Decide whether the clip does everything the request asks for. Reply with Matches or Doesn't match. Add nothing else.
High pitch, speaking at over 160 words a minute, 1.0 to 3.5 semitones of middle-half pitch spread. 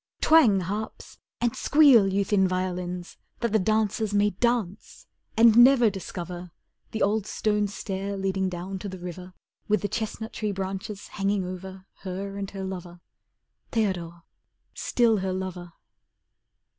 Doesn't match